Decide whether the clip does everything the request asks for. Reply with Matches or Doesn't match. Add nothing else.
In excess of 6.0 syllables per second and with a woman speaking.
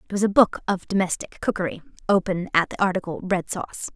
Matches